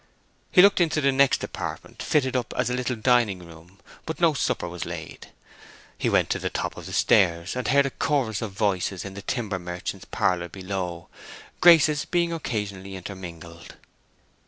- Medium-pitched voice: No, low, 105 Hz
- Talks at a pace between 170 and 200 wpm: Yes, average, 175 wpm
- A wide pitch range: Yes, wide, 7.0 semitones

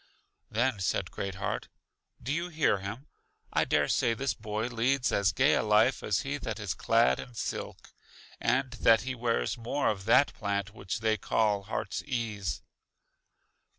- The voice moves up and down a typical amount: Yes, average, 3.6 semitones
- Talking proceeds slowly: No, average, 165 wpm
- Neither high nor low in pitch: No, low, 115 Hz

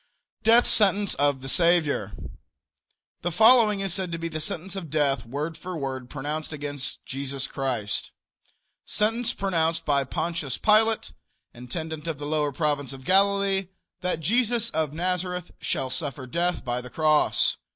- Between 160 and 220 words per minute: No, average, 150 wpm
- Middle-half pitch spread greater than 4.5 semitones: Yes, average, 5.2 semitones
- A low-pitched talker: No, medium, 160 Hz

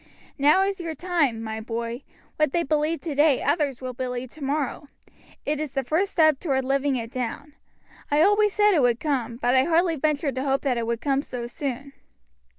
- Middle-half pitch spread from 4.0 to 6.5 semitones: No, average, 3.6 semitones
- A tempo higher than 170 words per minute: Yes, average, 195 wpm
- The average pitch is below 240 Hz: No, very high, 280 Hz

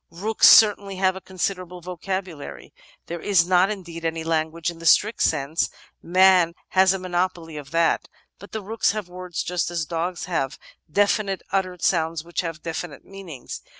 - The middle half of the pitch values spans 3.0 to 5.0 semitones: No, narrow, 2.5 semitones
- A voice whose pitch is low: No, medium, 180 Hz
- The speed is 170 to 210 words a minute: Yes, average, 175 wpm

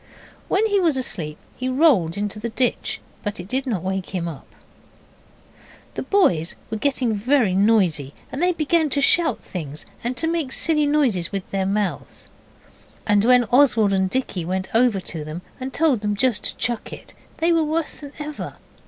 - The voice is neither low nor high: No, high, 230 Hz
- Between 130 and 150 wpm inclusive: No, average, 180 wpm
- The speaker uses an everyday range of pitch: No, wide, 7.3 semitones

